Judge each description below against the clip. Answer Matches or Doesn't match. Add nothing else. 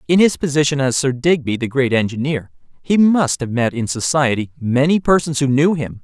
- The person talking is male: Matches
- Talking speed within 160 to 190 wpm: Doesn't match